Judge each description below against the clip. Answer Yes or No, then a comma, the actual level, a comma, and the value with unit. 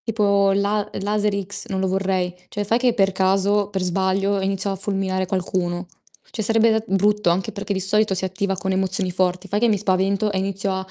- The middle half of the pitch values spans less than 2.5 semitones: Yes, narrow, 1.5 semitones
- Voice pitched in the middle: No, high, 195 Hz